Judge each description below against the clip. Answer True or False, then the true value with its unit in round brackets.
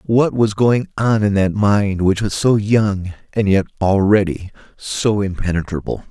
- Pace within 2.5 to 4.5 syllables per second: True (4.2 syllables/s)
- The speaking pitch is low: True (100 Hz)